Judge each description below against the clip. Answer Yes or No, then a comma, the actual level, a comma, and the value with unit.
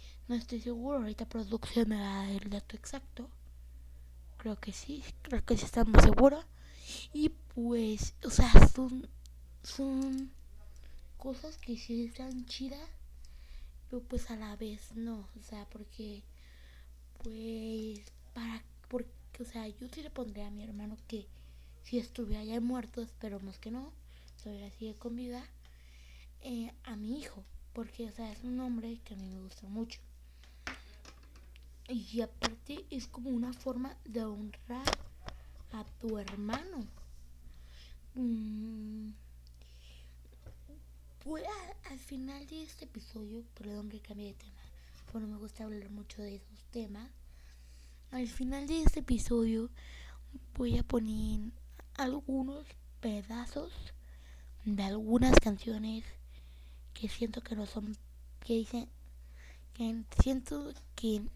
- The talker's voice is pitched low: No, high, 215 Hz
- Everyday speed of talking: No, slow, 130 wpm